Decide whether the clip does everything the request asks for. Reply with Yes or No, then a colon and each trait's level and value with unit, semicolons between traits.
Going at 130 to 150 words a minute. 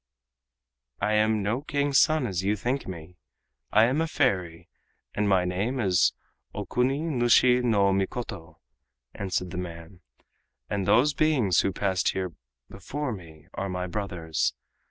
Yes: average, 140 wpm